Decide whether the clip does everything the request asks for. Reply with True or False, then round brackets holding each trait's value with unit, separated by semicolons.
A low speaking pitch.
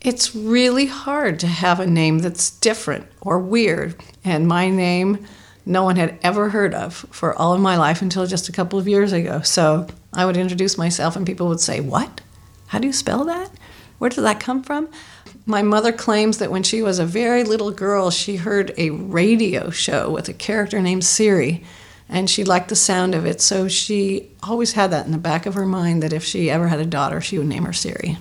False (190 Hz)